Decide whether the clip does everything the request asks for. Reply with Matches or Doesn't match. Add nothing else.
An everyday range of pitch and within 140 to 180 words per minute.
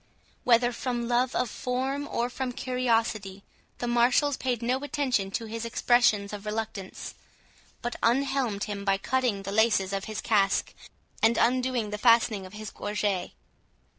Matches